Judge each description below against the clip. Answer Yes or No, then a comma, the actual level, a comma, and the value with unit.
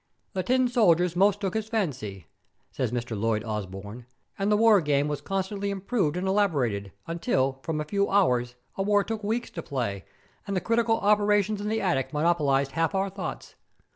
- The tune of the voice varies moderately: No, wide, 7.5 semitones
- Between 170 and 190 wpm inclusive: Yes, average, 180 wpm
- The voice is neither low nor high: Yes, medium, 180 Hz